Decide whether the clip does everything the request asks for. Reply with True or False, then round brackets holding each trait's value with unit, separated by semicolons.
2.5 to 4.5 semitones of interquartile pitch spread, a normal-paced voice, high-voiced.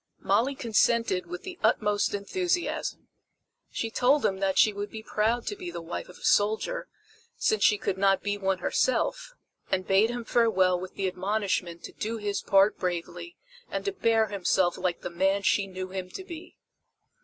True (4.2 semitones; 180 wpm; 205 Hz)